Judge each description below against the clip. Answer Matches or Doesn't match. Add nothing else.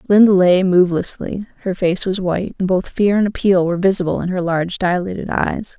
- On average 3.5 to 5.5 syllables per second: Doesn't match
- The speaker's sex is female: Matches